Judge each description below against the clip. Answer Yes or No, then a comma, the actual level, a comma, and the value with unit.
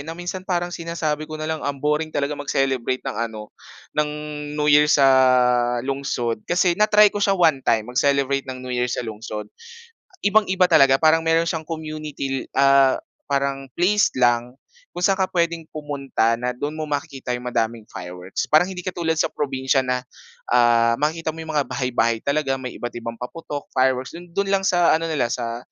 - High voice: No, medium, 140 Hz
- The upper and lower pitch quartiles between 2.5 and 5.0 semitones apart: Yes, average, 4.5 semitones